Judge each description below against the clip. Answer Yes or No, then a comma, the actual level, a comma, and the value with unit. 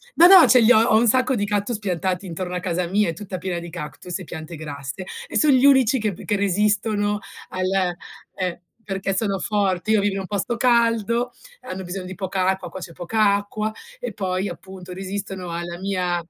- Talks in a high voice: Yes, high, 195 Hz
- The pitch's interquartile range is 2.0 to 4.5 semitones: Yes, average, 2.9 semitones